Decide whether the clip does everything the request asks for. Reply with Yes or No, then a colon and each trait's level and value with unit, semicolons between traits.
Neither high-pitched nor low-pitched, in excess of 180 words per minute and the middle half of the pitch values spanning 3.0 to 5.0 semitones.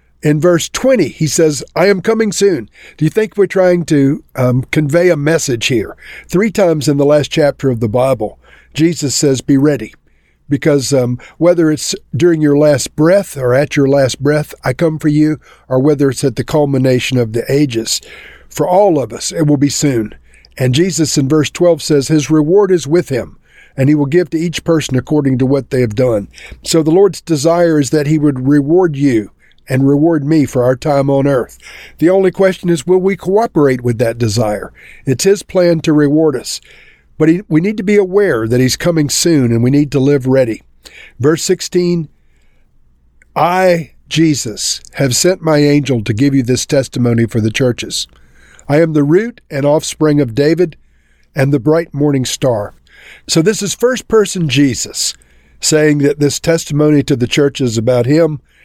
Yes: medium, 145 Hz; average, 190 wpm; average, 4.2 semitones